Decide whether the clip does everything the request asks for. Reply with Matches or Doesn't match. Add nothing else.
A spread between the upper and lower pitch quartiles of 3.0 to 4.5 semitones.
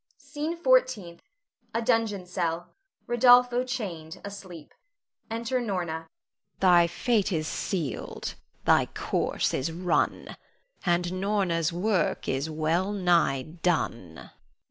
Doesn't match